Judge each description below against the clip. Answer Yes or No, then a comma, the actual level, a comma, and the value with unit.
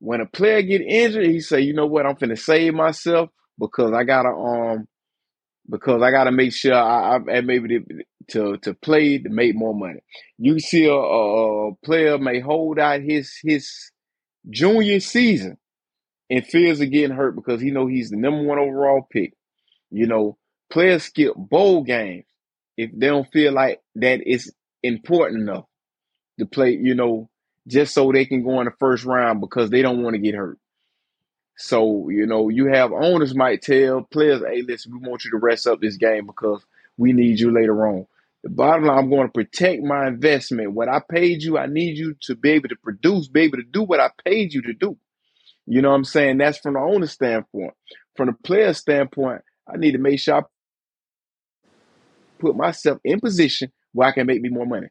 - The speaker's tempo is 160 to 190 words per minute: No, average, 200 wpm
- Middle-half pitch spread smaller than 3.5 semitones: No, average, 4.2 semitones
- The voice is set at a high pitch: No, low, 135 Hz